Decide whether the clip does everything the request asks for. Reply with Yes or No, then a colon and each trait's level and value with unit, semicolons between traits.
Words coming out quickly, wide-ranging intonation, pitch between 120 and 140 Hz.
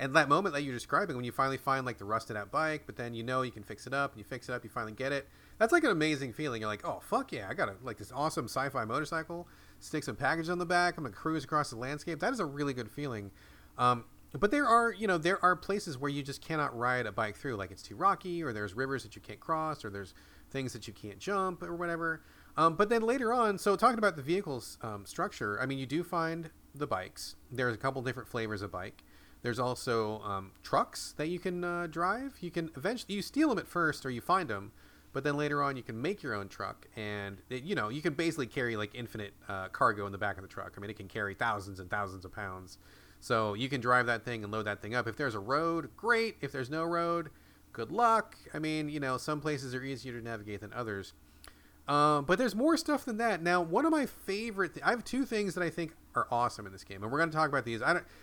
Yes: fast, 265 wpm; wide, 7.7 semitones; low, 135 Hz